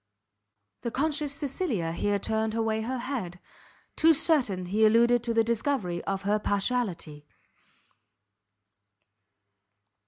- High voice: Yes, high, 225 Hz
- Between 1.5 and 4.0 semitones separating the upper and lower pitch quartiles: No, average, 4.5 semitones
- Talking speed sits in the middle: No, slow, 105 wpm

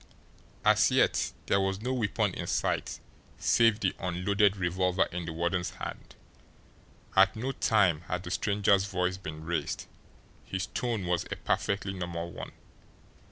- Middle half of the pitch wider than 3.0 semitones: No, narrow, 2.5 semitones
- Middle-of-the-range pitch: No, very low, 95 Hz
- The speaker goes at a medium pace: Yes, average, 145 wpm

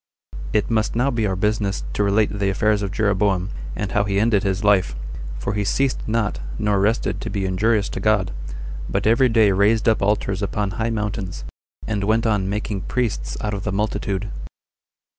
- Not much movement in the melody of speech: Yes, narrow, 1.8 semitones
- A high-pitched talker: No, low, 105 Hz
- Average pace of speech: Yes, average, 185 wpm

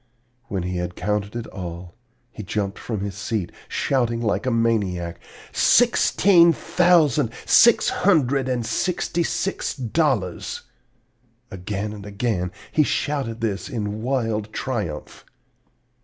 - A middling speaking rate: No, slow, 115 wpm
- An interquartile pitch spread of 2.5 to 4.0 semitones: No, wide, 5.4 semitones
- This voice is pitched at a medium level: No, low, 115 Hz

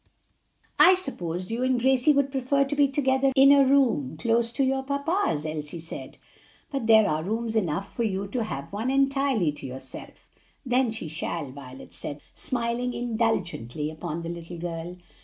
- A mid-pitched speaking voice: No, high, 225 Hz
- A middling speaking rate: Yes, average, 170 wpm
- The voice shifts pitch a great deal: Yes, wide, 8.2 semitones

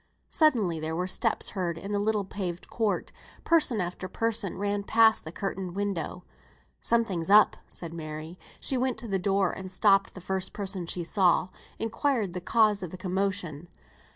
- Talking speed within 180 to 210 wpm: No, average, 170 wpm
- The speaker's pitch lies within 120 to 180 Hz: No, high, 195 Hz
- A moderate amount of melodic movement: Yes, average, 3.1 semitones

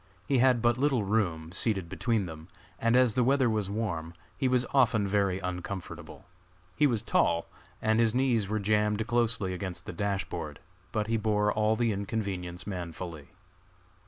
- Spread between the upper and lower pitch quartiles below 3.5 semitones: No, average, 4.0 semitones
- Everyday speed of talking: Yes, average, 165 wpm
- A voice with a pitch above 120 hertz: No, low, 105 Hz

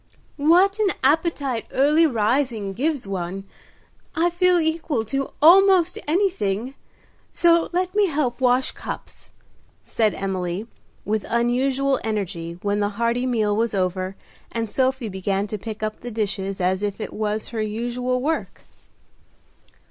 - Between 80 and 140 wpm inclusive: Yes, slow, 135 wpm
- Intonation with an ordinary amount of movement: No, wide, 6.5 semitones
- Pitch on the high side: Yes, high, 235 Hz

